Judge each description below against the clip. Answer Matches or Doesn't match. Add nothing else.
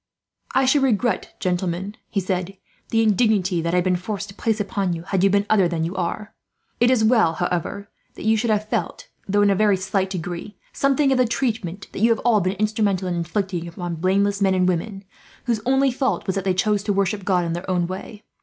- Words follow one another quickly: Matches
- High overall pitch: Matches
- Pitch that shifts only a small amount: Doesn't match